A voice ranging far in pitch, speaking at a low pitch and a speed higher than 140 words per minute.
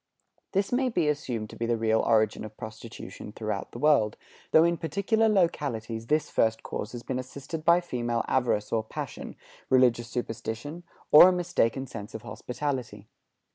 Yes: wide, 5.9 semitones; low, 125 Hz; average, 165 wpm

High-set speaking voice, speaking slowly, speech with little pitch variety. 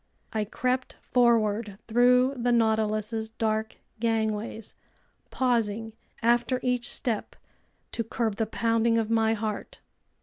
Yes: high, 225 Hz; slow, 110 wpm; narrow, 1.6 semitones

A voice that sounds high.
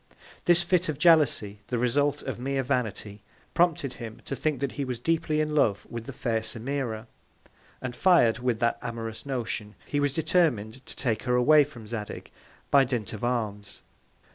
No: low, 125 Hz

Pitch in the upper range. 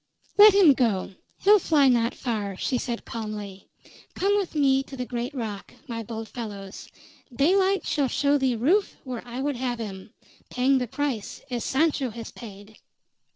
Yes: very high, 250 Hz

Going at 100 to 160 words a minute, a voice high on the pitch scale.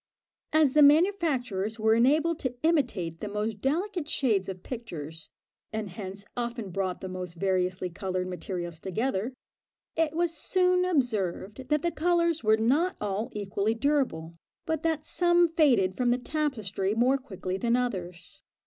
Yes: average, 150 wpm; high, 235 Hz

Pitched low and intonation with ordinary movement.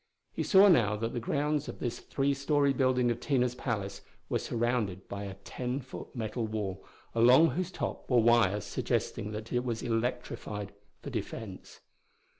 Yes: low, 120 Hz; average, 3.7 semitones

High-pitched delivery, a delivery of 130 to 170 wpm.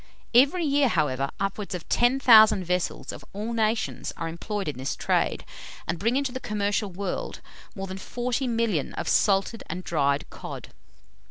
Yes: high, 205 Hz; average, 155 wpm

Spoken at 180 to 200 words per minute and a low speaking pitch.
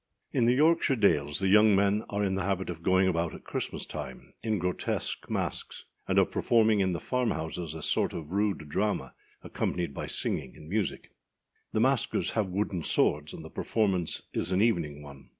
Yes: average, 190 wpm; very low, 95 Hz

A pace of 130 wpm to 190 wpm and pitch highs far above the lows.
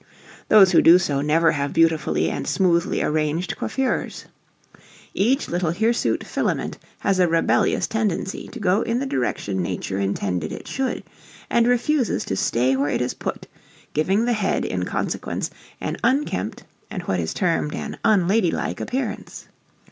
Yes: average, 150 wpm; wide, 7.2 semitones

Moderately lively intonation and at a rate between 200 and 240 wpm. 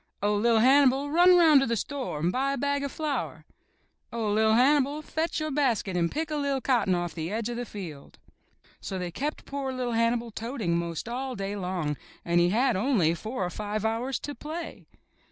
No: wide, 6.1 semitones; fast, 205 wpm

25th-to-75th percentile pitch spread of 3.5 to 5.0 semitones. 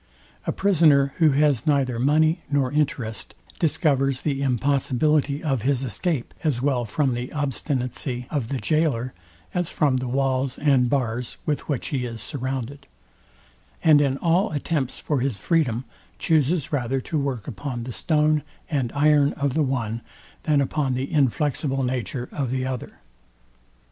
No: average, 2.9 semitones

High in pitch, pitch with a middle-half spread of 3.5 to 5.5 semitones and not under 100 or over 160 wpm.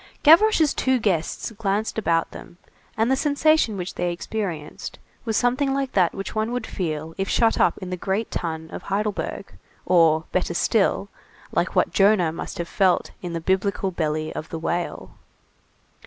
No: high, 195 Hz; average, 5.0 semitones; average, 170 wpm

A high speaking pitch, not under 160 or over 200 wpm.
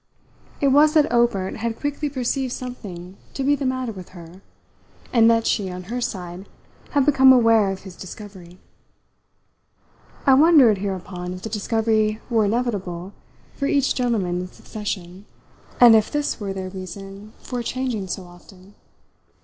No: high, 215 Hz; average, 150 wpm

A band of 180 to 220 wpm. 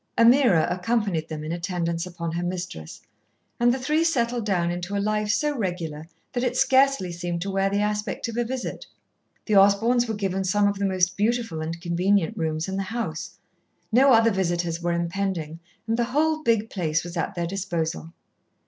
Yes: average, 185 wpm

